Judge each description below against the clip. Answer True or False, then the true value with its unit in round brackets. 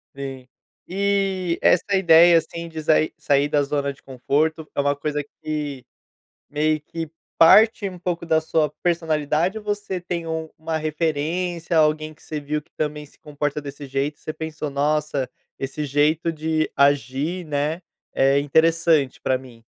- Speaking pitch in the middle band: True (155 Hz)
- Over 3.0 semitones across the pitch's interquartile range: False (2.5 semitones)